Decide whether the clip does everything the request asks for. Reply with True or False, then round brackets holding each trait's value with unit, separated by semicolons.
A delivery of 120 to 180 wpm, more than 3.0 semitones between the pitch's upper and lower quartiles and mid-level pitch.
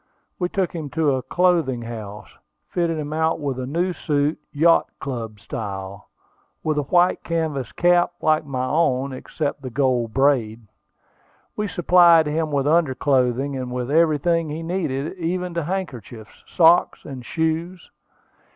True (150 wpm; 4.6 semitones; 150 Hz)